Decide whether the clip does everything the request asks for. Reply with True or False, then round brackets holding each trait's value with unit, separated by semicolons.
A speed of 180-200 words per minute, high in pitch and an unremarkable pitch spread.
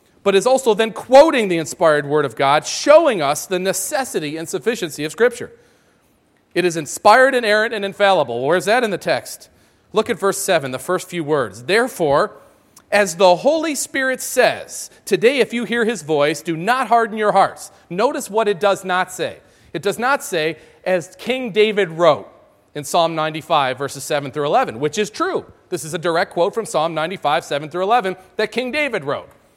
False (195 wpm; 195 Hz; 6.2 semitones)